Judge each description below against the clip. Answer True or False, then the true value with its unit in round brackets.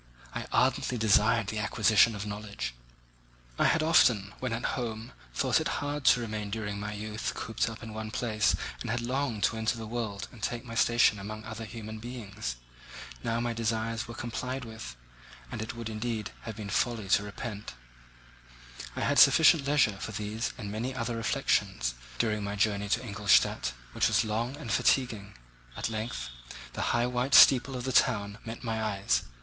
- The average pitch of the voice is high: False (110 Hz)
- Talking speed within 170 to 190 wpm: True (180 wpm)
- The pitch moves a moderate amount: False (2.3 semitones)